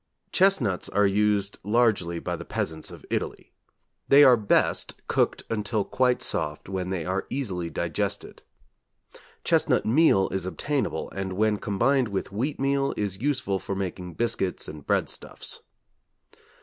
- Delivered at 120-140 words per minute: Yes, slow, 135 wpm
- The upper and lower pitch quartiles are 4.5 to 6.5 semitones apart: Yes, average, 4.8 semitones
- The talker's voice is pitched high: No, low, 105 Hz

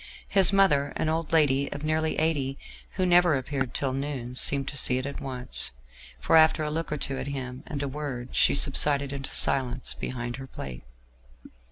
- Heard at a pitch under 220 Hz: Yes, medium, 140 Hz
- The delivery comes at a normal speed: Yes, average, 190 wpm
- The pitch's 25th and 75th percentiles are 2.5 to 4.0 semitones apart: Yes, average, 2.9 semitones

